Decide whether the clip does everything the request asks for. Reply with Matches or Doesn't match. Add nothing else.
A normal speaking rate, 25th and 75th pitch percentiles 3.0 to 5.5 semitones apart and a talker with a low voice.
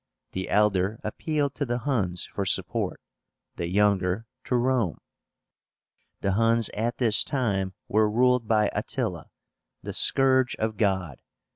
Doesn't match